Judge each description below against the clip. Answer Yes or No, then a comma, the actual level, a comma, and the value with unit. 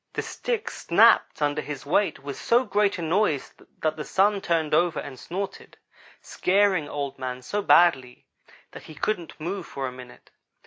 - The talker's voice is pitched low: No, medium, 165 Hz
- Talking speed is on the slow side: No, average, 170 wpm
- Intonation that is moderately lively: No, wide, 5.9 semitones